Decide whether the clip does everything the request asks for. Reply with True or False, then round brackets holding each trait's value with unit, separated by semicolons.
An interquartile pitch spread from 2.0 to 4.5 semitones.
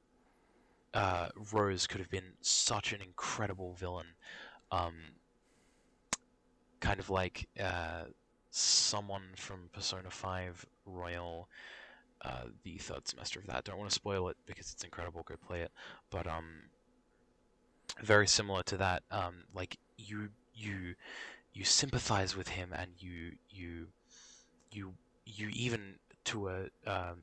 True (2.8 semitones)